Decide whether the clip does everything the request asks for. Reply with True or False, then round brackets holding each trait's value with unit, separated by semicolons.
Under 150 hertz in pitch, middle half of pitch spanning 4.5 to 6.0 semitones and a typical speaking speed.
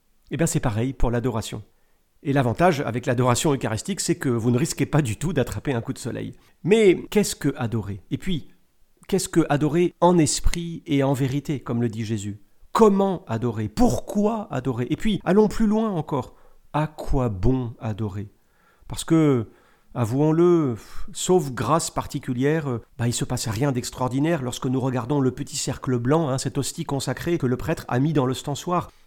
True (140 Hz; 5.0 semitones; 180 wpm)